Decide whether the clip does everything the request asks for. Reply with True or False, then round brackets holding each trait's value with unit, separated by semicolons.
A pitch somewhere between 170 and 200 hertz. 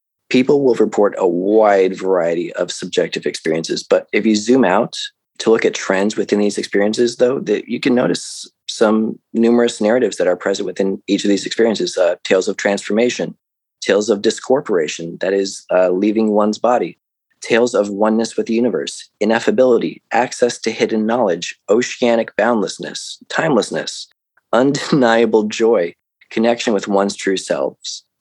False (110 Hz)